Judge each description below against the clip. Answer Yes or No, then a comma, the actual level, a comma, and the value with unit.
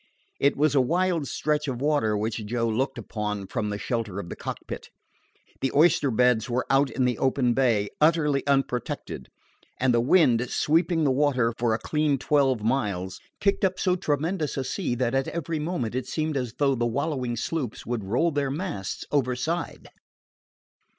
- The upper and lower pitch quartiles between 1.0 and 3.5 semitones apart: No, average, 4.3 semitones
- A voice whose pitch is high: No, low, 135 Hz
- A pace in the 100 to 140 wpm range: No, average, 175 wpm